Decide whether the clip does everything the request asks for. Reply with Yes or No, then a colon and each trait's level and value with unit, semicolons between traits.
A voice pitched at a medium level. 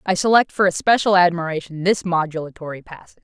Yes: medium, 175 Hz